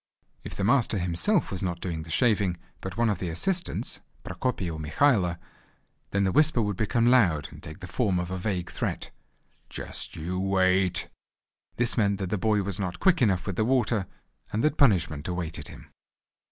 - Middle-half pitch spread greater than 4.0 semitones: Yes, average, 4.5 semitones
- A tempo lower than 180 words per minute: No, average, 185 wpm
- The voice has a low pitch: Yes, very low, 95 Hz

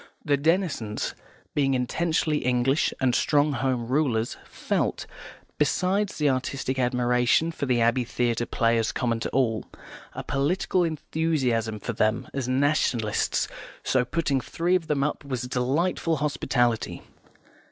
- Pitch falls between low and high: No, low, 130 Hz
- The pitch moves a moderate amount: Yes, average, 3.8 semitones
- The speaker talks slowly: Yes, slow, 130 wpm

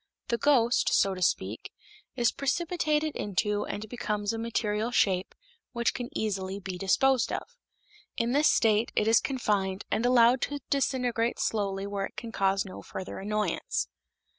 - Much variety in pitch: No, average, 3.9 semitones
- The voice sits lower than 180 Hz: No, high, 225 Hz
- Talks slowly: No, average, 155 wpm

